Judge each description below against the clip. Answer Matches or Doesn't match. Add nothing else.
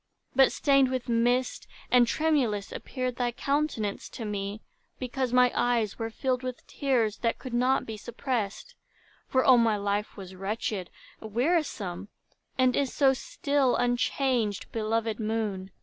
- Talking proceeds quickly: Doesn't match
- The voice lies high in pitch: Matches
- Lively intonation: Doesn't match